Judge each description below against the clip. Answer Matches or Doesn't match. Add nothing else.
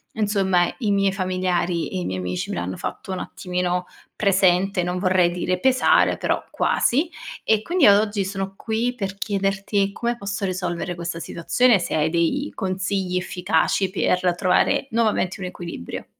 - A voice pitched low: Doesn't match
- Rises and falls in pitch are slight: Matches